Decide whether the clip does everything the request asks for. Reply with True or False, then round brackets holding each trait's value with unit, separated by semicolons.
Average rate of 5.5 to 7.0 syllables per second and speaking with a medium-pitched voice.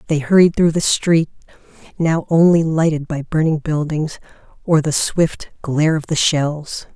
False (4.4 syllables/s; 155 Hz)